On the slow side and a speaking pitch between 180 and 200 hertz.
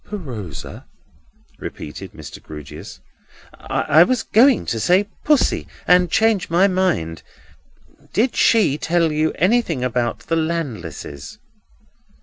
No: slow, 105 wpm; medium, 165 Hz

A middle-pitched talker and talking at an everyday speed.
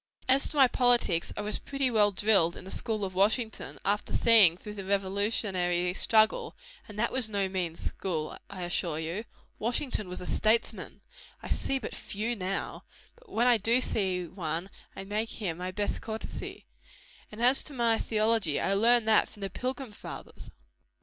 No: high, 210 Hz; average, 175 wpm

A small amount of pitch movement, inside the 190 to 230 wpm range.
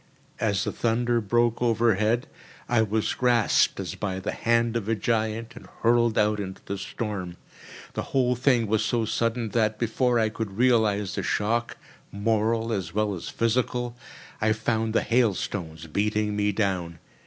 No: narrow, 2.2 semitones; average, 160 wpm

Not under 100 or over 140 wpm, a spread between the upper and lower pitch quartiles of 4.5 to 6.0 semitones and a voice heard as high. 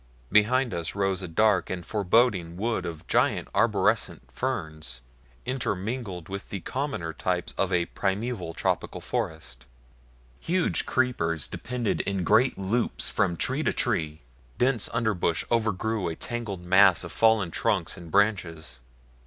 No: slow, 135 wpm; average, 5.3 semitones; very low, 95 Hz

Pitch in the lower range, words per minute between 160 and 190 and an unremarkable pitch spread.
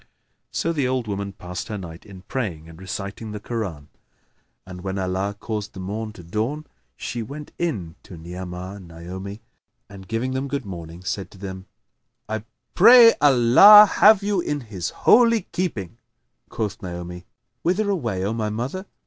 No: low, 105 Hz; average, 165 wpm; wide, 6.1 semitones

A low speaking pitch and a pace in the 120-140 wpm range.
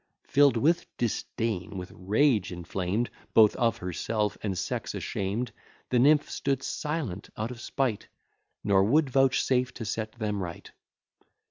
Yes: low, 115 Hz; slow, 135 wpm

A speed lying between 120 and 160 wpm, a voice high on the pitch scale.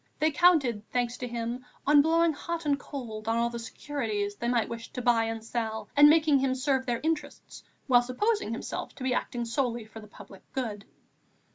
No: average, 200 wpm; high, 245 Hz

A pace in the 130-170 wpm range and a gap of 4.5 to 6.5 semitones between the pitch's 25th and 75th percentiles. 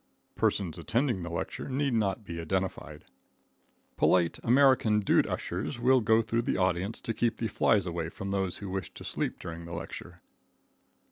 Yes: average, 165 wpm; average, 4.9 semitones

